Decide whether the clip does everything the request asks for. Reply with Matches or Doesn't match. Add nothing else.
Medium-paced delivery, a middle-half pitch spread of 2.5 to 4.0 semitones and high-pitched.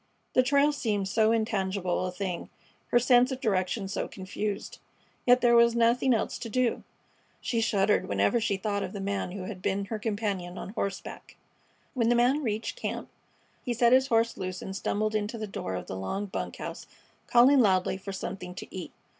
Matches